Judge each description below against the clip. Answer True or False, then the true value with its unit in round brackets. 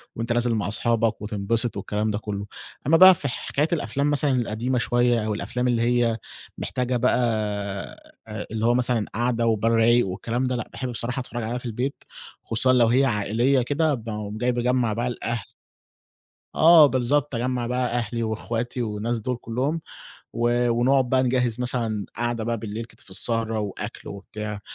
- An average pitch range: False (2.1 semitones)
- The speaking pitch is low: True (120 Hz)